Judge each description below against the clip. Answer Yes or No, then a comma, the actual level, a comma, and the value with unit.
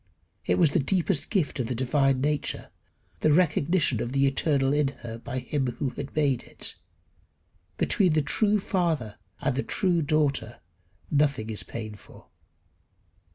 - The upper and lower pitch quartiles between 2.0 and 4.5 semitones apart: Yes, average, 3.3 semitones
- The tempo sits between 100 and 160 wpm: Yes, average, 150 wpm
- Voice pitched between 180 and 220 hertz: No, medium, 140 Hz